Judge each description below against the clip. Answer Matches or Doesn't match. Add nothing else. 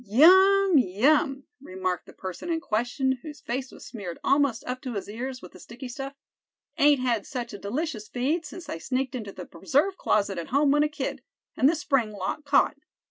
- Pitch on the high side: Matches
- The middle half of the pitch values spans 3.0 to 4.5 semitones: Doesn't match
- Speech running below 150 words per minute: Doesn't match